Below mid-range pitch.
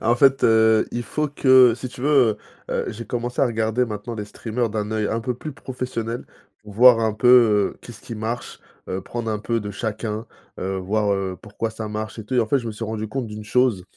Yes: low, 115 Hz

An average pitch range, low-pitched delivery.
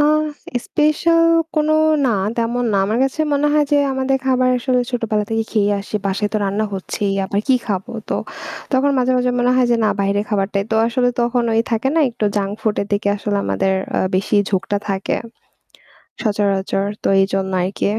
No: average, 4.1 semitones; high, 220 Hz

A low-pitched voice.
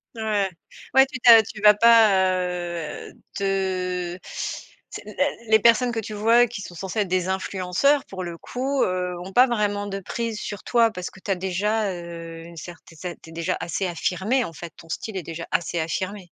No: high, 190 Hz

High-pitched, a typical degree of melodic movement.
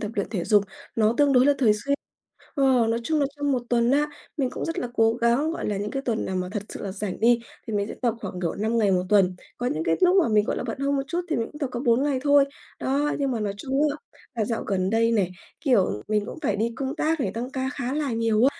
Yes: high, 235 Hz; average, 4.7 semitones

